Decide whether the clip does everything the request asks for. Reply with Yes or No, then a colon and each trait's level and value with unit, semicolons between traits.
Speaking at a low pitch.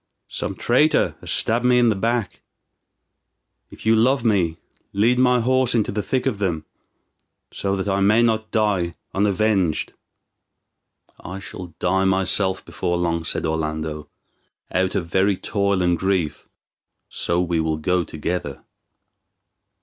Yes: very low, 95 Hz